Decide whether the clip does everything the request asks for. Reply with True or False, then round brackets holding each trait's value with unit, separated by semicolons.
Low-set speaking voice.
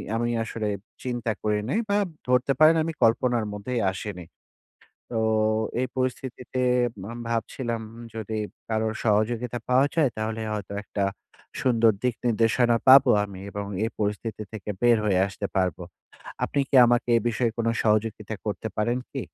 True (115 Hz)